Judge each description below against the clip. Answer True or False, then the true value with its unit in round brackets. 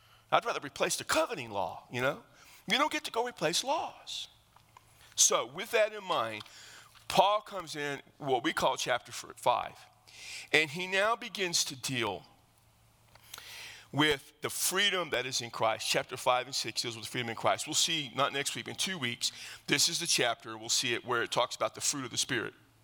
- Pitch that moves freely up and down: True (7.3 semitones)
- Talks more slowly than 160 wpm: False (195 wpm)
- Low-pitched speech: False (150 Hz)